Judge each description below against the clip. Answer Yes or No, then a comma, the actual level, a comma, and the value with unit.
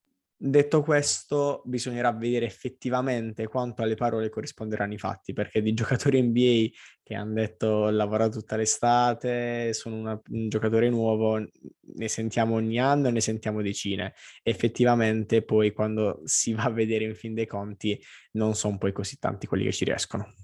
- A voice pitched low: Yes, low, 110 Hz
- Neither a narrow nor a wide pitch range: No, narrow, 1.9 semitones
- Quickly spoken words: No, average, 160 wpm